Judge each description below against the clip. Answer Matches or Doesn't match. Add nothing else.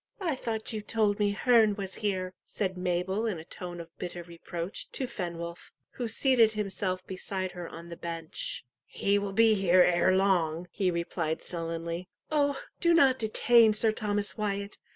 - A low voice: Doesn't match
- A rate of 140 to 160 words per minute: Doesn't match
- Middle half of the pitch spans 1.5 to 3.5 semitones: Doesn't match